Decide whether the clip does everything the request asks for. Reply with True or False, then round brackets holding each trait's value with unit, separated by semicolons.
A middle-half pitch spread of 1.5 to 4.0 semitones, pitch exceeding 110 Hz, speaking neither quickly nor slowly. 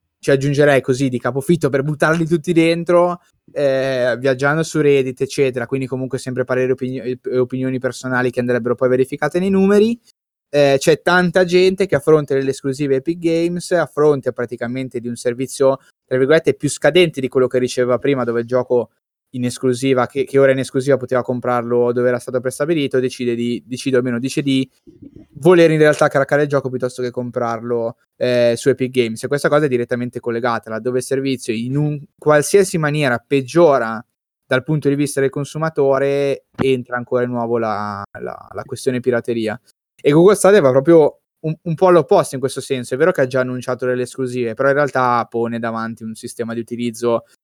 False (2.9 semitones; 130 Hz; 185 wpm)